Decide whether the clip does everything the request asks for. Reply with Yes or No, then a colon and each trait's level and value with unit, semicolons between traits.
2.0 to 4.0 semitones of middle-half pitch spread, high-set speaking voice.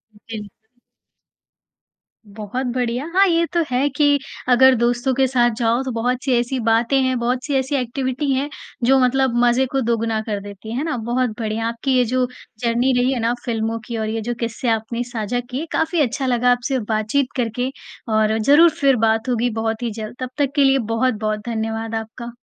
Yes: average, 2.7 semitones; high, 245 Hz